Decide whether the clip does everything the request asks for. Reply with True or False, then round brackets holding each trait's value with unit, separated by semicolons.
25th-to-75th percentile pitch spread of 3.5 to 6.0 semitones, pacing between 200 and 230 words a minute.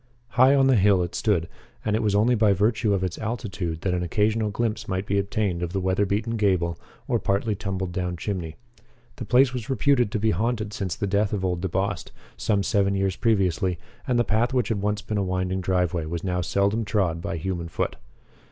False (3.0 semitones; 205 wpm)